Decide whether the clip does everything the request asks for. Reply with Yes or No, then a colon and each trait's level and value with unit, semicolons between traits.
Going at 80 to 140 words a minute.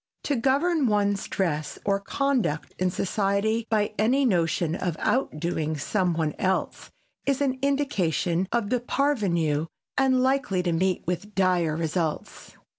Yes: slow, 135 wpm